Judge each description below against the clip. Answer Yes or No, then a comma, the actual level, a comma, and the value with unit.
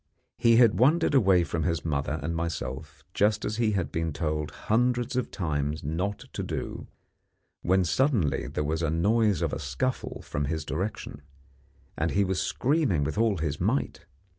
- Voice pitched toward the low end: Yes, very low, 90 Hz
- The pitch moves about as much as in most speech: No, wide, 6.4 semitones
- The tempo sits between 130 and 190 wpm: Yes, average, 170 wpm